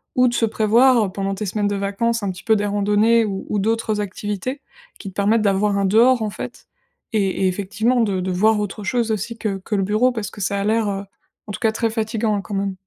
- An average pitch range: No, narrow, 2.3 semitones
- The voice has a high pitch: Yes, high, 210 Hz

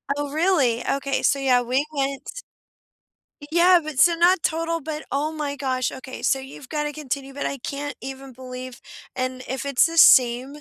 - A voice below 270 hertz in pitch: No, very high, 275 Hz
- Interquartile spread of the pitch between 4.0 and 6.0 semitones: No, average, 2.9 semitones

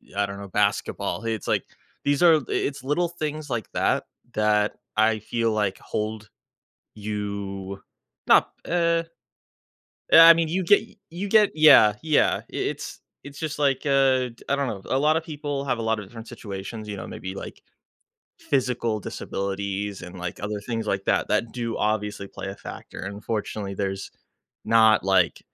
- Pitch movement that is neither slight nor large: No, wide, 5.8 semitones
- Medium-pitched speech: No, low, 110 Hz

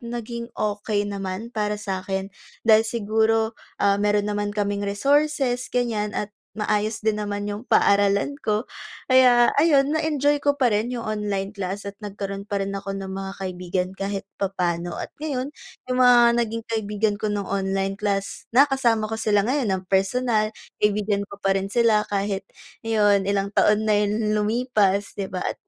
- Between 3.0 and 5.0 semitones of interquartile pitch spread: No, narrow, 2.4 semitones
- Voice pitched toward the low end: No, high, 210 Hz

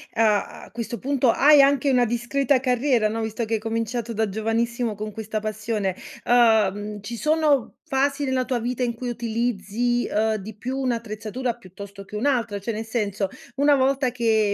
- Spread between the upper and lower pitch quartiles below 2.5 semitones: No, average, 2.8 semitones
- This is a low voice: No, high, 230 Hz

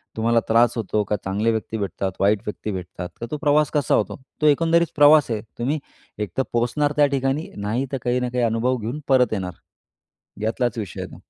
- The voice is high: No, low, 120 Hz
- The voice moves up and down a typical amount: Yes, average, 4.8 semitones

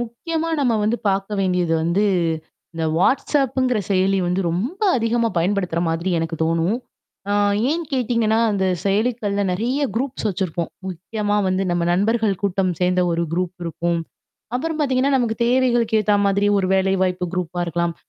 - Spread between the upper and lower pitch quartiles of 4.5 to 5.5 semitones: Yes, average, 4.8 semitones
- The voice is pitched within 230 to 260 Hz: No, high, 200 Hz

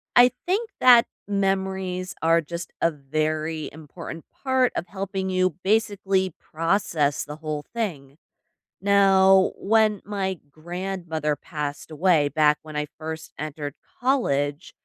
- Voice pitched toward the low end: No, medium, 175 Hz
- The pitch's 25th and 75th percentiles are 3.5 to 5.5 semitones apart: Yes, average, 4.2 semitones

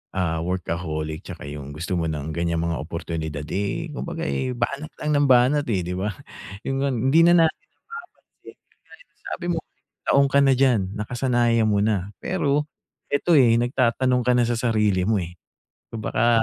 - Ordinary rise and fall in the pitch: No, wide, 7.2 semitones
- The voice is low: Yes, low, 110 Hz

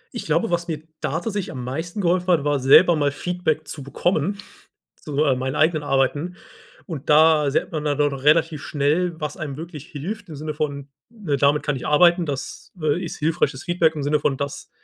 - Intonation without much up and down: No, average, 3.2 semitones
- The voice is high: No, medium, 155 Hz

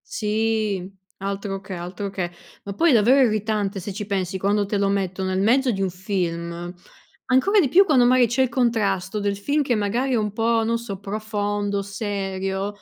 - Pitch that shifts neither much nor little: Yes, average, 3.0 semitones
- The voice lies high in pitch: Yes, high, 205 Hz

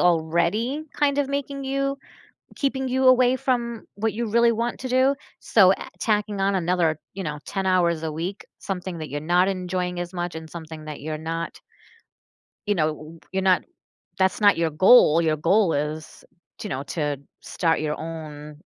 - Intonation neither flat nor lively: No, wide, 6.2 semitones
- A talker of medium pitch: Yes, medium, 180 Hz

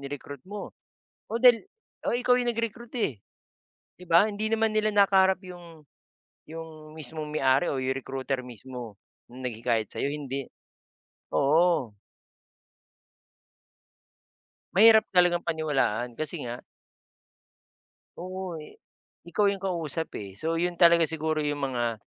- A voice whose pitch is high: No, medium, 160 Hz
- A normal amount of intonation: No, wide, 6.2 semitones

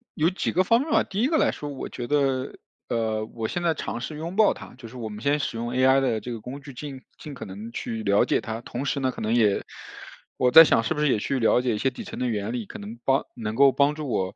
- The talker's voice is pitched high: No, low, 130 Hz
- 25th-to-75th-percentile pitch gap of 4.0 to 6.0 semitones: Yes, average, 4.4 semitones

